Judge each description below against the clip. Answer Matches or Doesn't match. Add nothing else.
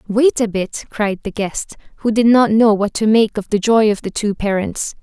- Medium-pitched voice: Doesn't match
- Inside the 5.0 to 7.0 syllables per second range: Doesn't match